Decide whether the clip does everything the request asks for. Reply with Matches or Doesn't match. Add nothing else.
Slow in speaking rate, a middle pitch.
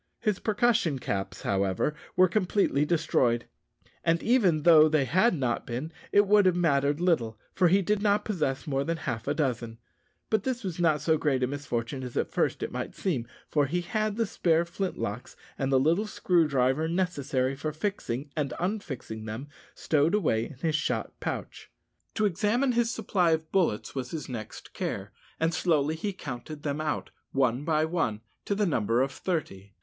Doesn't match